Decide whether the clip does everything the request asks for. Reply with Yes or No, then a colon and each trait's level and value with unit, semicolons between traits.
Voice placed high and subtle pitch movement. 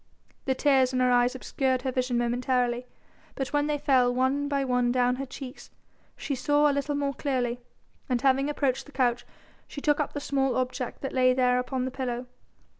Yes: very high, 260 Hz; narrow, 1.9 semitones